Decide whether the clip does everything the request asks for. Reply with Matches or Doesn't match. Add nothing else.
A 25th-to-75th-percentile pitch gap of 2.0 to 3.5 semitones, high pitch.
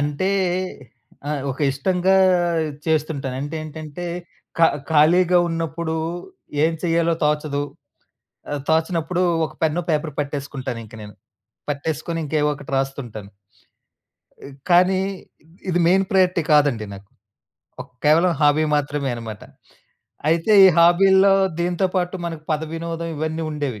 Doesn't match